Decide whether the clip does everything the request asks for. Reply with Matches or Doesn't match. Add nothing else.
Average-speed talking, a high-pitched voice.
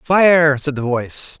Doesn't match